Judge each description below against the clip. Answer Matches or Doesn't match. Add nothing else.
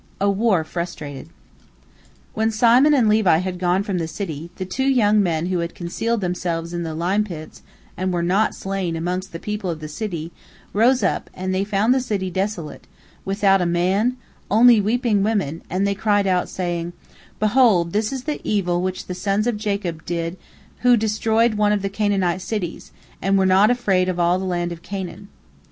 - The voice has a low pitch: Doesn't match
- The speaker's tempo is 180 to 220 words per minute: Matches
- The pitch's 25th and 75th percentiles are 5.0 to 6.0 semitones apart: Doesn't match